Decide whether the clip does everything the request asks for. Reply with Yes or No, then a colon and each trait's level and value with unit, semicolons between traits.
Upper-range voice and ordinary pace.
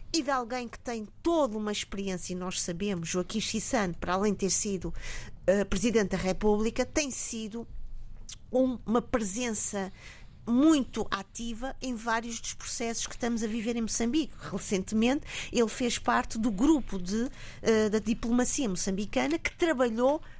Yes: high, 230 Hz; average, 155 wpm